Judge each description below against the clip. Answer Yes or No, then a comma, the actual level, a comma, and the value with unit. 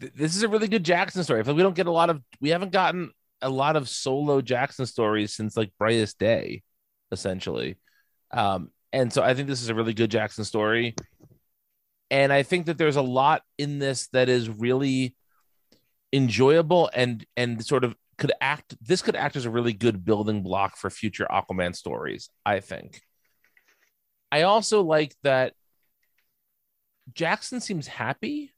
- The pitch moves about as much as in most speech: No, wide, 6.4 semitones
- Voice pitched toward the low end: Yes, low, 130 Hz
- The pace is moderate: Yes, average, 170 wpm